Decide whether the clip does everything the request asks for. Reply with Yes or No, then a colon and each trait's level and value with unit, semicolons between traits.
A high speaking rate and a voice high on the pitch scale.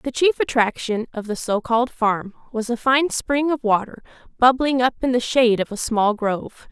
No: average, 195 wpm; high, 240 Hz